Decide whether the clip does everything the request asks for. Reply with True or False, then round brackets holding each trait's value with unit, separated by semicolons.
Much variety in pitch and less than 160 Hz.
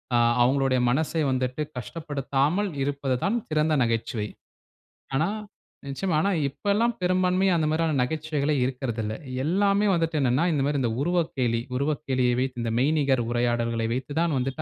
False (4.4 semitones; 140 Hz)